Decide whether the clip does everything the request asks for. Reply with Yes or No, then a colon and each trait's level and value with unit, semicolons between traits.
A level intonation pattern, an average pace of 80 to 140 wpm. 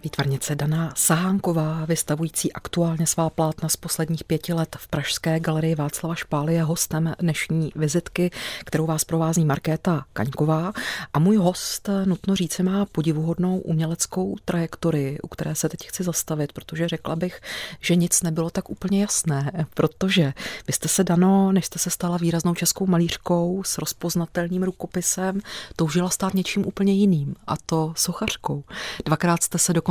No: narrow, 2.3 semitones; average, 155 wpm